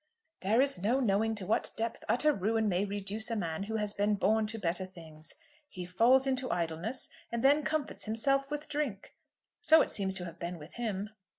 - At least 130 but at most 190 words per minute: No, average, 200 wpm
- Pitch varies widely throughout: No, average, 5.0 semitones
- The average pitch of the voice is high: Yes, high, 215 Hz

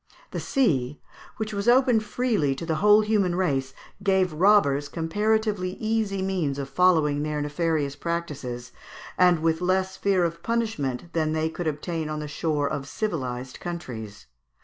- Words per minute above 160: No, average, 150 wpm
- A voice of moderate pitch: Yes, medium, 170 Hz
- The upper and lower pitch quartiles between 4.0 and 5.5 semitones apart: Yes, average, 5.2 semitones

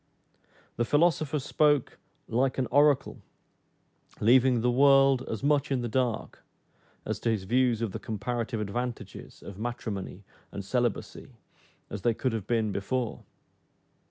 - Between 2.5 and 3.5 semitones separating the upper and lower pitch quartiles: Yes, average, 3.2 semitones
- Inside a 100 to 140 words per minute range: Yes, slow, 135 wpm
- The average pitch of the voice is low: Yes, low, 120 Hz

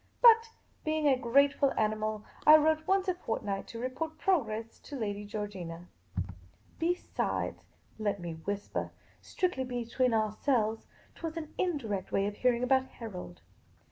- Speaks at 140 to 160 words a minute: Yes, average, 155 wpm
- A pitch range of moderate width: No, wide, 6.7 semitones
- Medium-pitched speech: No, high, 240 Hz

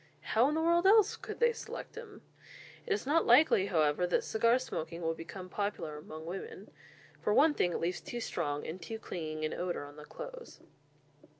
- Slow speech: No, average, 195 wpm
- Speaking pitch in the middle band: No, high, 195 Hz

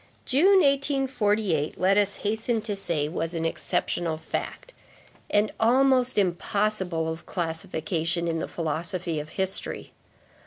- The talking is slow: Yes, slow, 120 wpm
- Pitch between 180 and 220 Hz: Yes, high, 190 Hz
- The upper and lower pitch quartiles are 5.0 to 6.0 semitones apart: Yes, average, 5.3 semitones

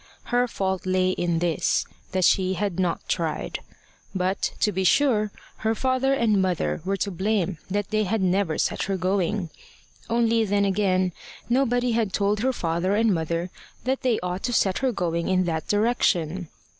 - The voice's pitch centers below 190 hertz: No, high, 195 Hz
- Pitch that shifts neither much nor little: Yes, average, 3.5 semitones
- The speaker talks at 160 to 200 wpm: Yes, average, 170 wpm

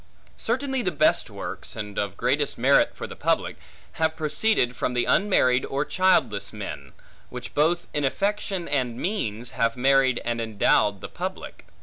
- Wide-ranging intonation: Yes, wide, 6.9 semitones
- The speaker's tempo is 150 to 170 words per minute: Yes, average, 155 wpm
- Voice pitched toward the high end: No, low, 135 Hz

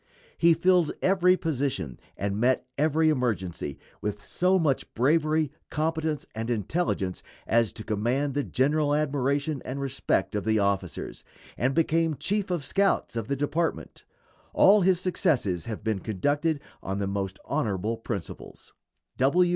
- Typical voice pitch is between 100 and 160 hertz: Yes, medium, 140 Hz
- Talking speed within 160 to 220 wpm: No, average, 140 wpm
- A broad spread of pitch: Yes, wide, 6.6 semitones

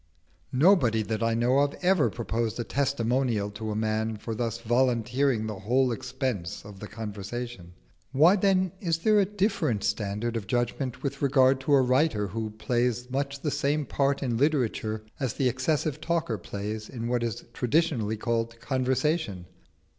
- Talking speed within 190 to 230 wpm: No, average, 160 wpm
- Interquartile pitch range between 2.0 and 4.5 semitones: Yes, average, 4.0 semitones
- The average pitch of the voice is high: No, low, 120 Hz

